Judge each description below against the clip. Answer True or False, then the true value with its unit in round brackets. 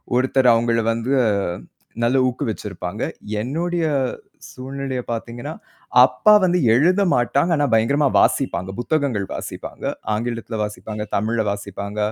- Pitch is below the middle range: True (120 Hz)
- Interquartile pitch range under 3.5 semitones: False (4.1 semitones)